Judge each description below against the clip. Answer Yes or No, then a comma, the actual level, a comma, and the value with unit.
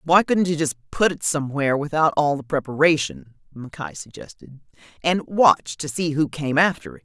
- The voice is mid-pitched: Yes, medium, 150 Hz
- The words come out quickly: No, average, 180 wpm